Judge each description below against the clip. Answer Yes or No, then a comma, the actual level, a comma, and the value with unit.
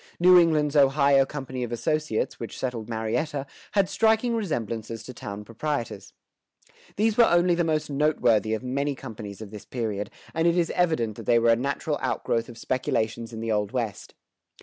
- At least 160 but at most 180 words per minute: Yes, average, 175 wpm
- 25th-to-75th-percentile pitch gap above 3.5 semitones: Yes, wide, 5.4 semitones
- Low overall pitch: Yes, low, 130 Hz